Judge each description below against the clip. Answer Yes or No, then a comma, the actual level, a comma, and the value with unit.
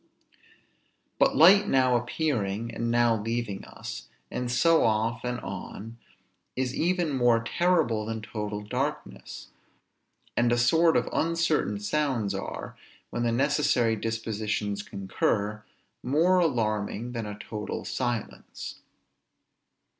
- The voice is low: Yes, low, 120 Hz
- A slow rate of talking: Yes, slow, 115 wpm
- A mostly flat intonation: No, average, 4.4 semitones